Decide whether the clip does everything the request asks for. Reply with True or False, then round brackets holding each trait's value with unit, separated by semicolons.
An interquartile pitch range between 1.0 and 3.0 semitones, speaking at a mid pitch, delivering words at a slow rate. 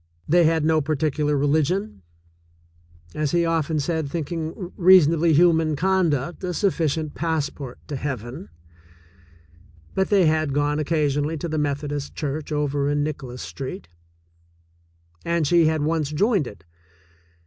True (2.4 semitones; 155 Hz; 130 wpm)